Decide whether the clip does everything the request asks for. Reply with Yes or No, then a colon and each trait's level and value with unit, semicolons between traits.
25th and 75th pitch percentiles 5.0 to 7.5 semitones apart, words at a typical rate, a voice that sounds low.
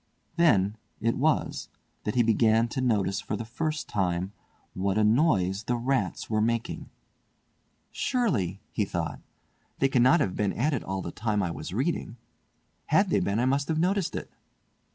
Yes: average, 5.3 semitones; average, 170 wpm; low, 115 Hz